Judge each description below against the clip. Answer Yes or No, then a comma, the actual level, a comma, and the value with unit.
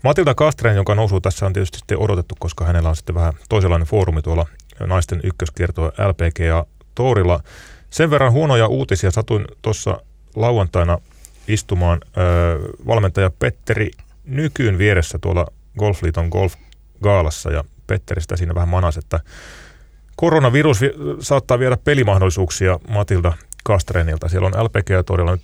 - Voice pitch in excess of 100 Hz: No, very low, 95 Hz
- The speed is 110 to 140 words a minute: Yes, average, 130 wpm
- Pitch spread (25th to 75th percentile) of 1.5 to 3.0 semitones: No, average, 4.3 semitones